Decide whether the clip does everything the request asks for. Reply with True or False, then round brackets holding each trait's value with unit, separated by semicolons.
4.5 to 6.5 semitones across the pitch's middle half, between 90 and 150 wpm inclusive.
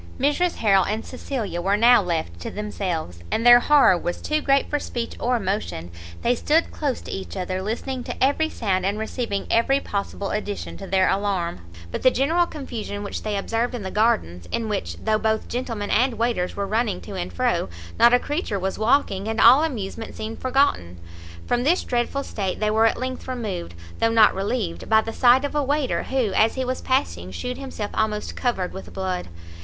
False (4.8 semitones; 200 wpm)